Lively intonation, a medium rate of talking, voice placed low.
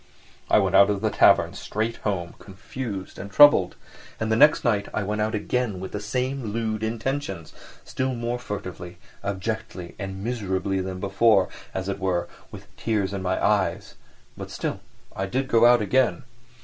No: average, 3.6 semitones; average, 165 wpm; low, 105 Hz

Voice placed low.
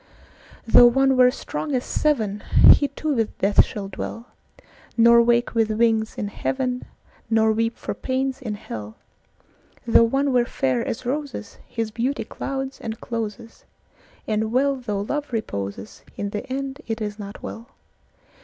No: high, 230 Hz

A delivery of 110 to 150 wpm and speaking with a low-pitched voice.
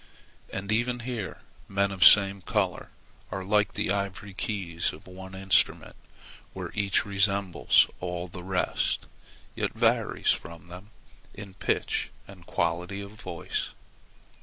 Yes: slow, 135 wpm; very low, 95 Hz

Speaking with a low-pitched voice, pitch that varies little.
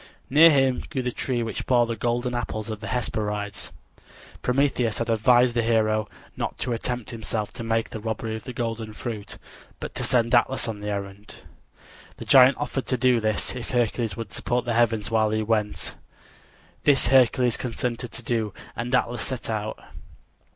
Yes: low, 115 Hz; narrow, 2.3 semitones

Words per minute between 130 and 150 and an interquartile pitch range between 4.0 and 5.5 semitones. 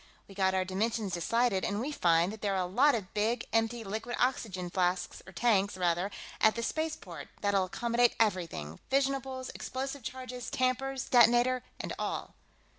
No: average, 165 wpm; average, 4.9 semitones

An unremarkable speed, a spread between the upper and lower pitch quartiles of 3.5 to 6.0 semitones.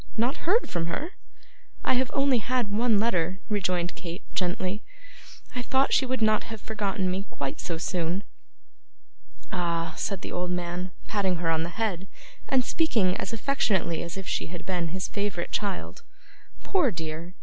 Yes: average, 165 wpm; average, 4.4 semitones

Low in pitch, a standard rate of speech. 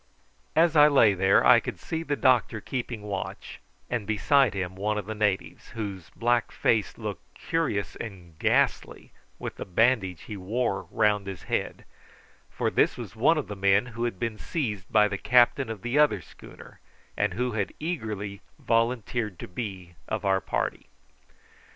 Yes: low, 110 Hz; average, 170 wpm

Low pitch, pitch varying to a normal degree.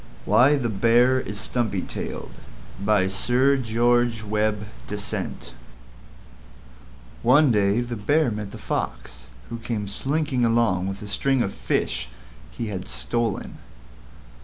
Yes: low, 110 Hz; average, 3.5 semitones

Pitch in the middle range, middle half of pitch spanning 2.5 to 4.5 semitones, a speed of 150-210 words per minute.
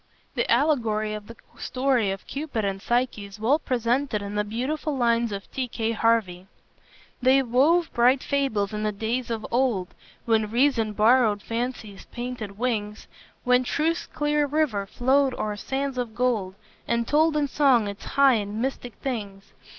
No: high, 235 Hz; average, 3.9 semitones; average, 160 wpm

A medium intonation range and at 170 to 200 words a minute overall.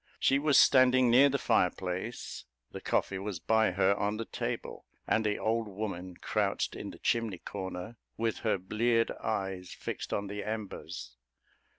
No: average, 3.5 semitones; average, 160 wpm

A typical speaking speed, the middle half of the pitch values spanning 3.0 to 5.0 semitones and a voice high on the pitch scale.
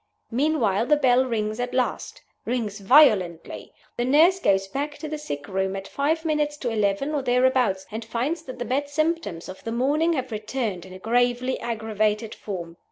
No: average, 180 wpm; wide, 5.6 semitones; high, 245 Hz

